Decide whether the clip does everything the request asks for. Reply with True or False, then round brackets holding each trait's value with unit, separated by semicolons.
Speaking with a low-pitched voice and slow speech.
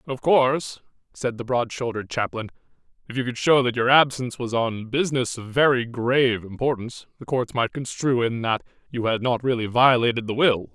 False (125 Hz; 190 wpm)